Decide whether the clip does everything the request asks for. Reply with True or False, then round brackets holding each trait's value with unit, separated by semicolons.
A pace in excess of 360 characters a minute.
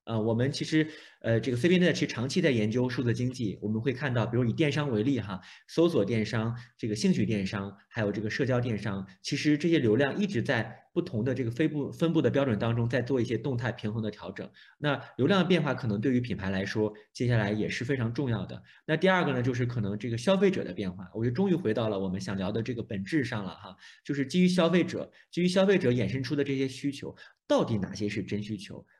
True (370 characters per minute)